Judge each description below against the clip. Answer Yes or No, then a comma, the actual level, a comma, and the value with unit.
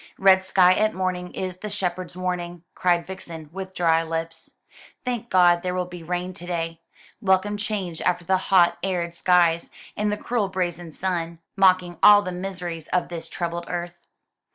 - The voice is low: No, medium, 180 Hz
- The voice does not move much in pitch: Yes, narrow, 1.7 semitones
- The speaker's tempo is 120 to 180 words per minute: Yes, average, 170 wpm